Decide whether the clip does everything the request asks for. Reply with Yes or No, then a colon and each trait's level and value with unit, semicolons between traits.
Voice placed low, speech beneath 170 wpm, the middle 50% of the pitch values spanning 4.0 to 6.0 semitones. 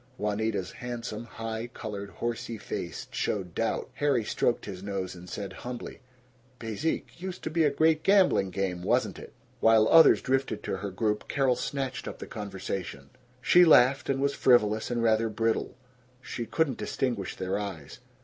Yes: low, 115 Hz; average, 160 wpm; average, 4.8 semitones